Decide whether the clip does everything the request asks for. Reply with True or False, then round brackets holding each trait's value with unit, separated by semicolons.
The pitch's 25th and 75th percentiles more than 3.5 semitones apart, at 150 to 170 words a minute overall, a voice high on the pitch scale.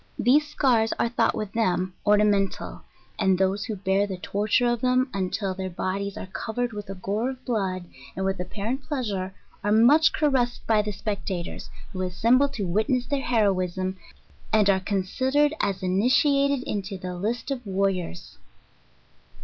True (4.4 semitones; 165 wpm; 205 Hz)